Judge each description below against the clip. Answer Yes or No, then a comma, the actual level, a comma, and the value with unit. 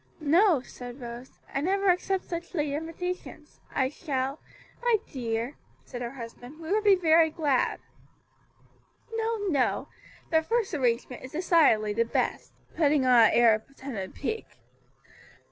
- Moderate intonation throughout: No, wide, 6.3 semitones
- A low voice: No, very high, 285 Hz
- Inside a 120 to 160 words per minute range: Yes, average, 145 wpm